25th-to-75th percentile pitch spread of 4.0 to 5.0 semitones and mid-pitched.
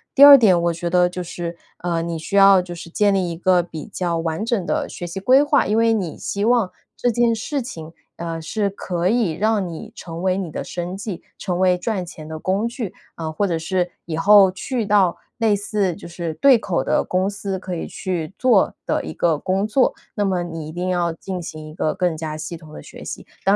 No: average, 3.4 semitones; medium, 180 Hz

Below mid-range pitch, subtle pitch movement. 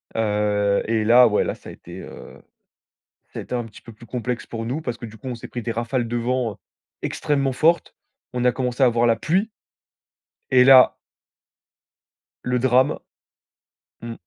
Yes: low, 120 Hz; narrow, 2.1 semitones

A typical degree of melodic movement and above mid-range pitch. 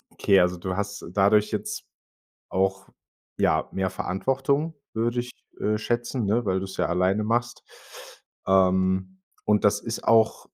No: average, 3.5 semitones; low, 100 Hz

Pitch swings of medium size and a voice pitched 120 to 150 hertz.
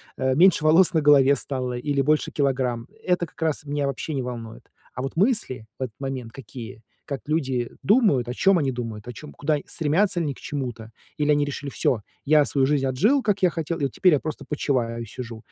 Yes: average, 3.8 semitones; medium, 140 Hz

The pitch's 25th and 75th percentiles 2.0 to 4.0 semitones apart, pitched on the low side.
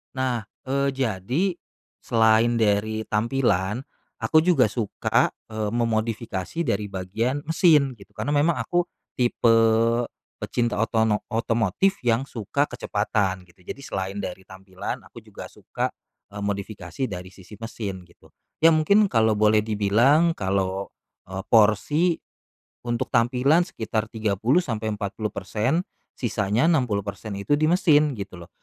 No: average, 4.7 semitones; low, 110 Hz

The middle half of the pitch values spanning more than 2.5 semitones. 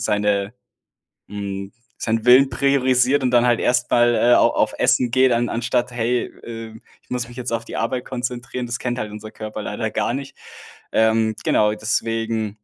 No: narrow, 2.2 semitones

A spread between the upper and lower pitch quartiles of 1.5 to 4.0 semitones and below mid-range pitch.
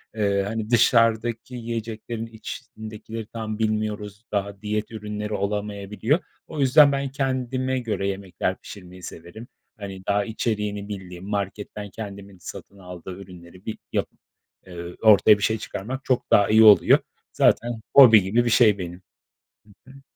Yes: narrow, 2.6 semitones; low, 105 Hz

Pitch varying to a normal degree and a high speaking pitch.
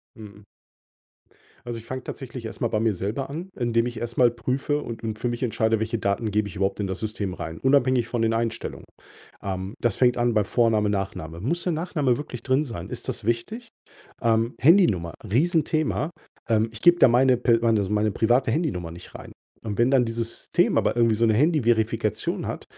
No: average, 3.3 semitones; low, 115 Hz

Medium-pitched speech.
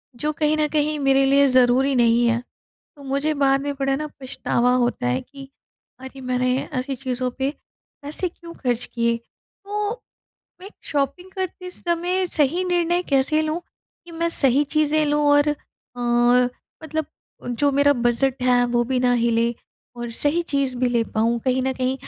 No: very high, 275 Hz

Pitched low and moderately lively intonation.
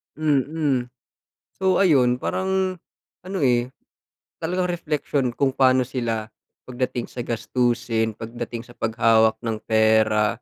Yes: low, 125 Hz; average, 4.6 semitones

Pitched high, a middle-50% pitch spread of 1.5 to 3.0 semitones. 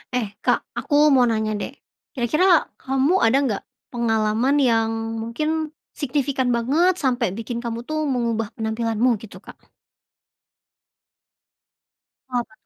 No: high, 245 Hz; average, 3.8 semitones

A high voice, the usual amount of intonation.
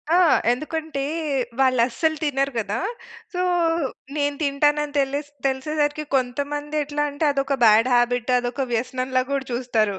Yes: very high, 275 Hz; average, 3.0 semitones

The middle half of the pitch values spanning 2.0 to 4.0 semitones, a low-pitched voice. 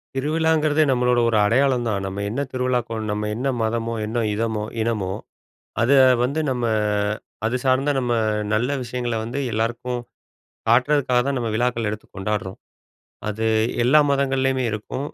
Yes: average, 3.0 semitones; low, 120 Hz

